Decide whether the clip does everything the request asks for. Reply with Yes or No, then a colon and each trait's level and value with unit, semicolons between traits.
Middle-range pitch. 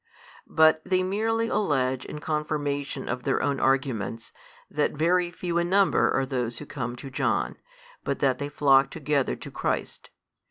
Yes: medium, 145 Hz